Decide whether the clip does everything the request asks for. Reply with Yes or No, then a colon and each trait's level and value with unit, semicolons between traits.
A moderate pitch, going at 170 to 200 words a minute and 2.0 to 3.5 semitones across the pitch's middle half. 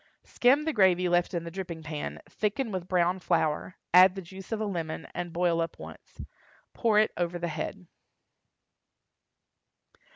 No: medium, 180 Hz; average, 160 wpm; narrow, 2.5 semitones